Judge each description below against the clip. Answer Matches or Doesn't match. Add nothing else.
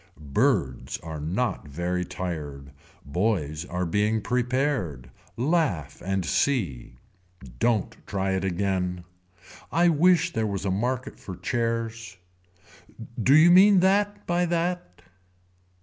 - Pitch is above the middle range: Doesn't match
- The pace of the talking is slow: Matches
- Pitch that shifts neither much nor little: Doesn't match